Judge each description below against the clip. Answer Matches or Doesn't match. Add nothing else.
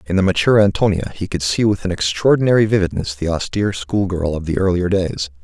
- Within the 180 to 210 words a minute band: Matches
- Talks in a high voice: Doesn't match